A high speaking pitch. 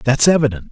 No: low, 135 Hz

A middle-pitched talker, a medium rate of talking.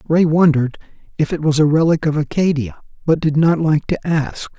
Yes: medium, 155 Hz; average, 195 wpm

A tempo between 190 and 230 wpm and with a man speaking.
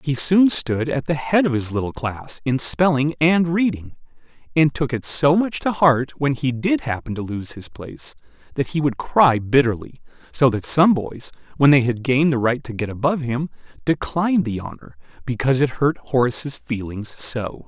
Yes: average, 195 wpm; male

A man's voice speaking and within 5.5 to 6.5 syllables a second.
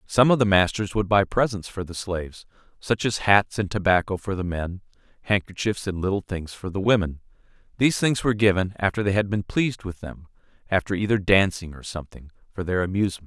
Yes: male; 5.9 syllables/s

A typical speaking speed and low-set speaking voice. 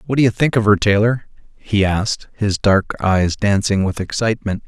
Yes: average, 195 wpm; low, 105 Hz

